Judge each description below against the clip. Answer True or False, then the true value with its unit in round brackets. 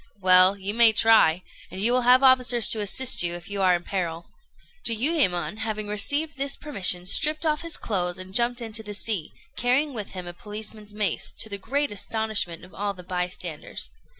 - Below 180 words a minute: False (190 wpm)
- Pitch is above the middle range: True (210 Hz)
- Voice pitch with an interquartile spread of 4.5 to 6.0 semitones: True (5.0 semitones)